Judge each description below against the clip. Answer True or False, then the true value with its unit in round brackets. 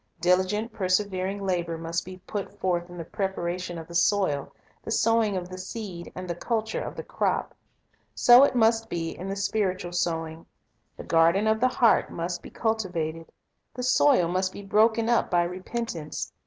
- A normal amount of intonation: True (4.1 semitones)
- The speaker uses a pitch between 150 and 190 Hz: True (185 Hz)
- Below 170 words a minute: False (175 wpm)